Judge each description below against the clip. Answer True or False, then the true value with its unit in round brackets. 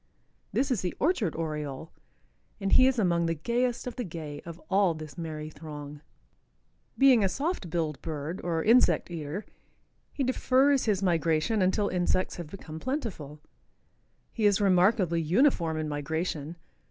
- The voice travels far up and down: True (5.9 semitones)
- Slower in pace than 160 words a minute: True (150 wpm)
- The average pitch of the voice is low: False (175 Hz)